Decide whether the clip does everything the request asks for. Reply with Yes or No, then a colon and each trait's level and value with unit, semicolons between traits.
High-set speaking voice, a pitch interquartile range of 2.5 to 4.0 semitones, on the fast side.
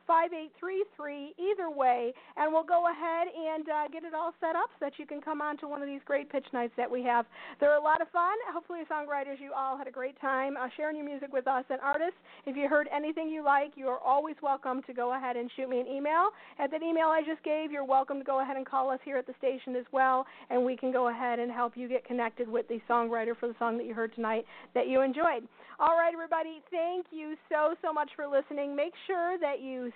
Yes: very high, 280 Hz; average, 3.6 semitones; fast, 250 wpm